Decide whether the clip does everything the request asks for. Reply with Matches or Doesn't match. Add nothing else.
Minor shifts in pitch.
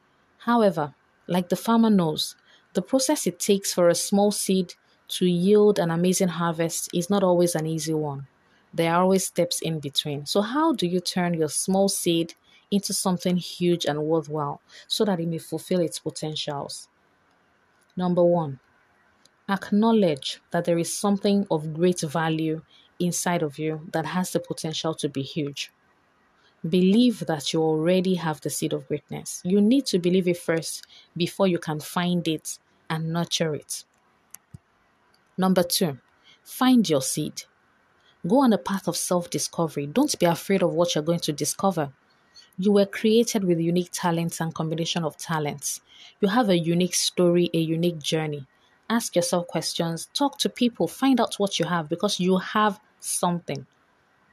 Doesn't match